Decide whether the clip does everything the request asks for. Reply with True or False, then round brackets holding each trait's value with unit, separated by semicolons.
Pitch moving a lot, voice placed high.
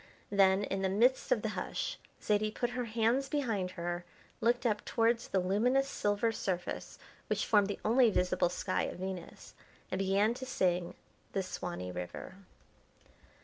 False (4.0 semitones; 205 Hz)